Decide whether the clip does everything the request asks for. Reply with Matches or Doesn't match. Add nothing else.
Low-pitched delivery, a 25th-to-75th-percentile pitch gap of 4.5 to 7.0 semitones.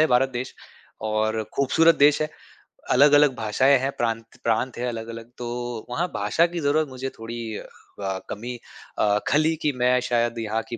Doesn't match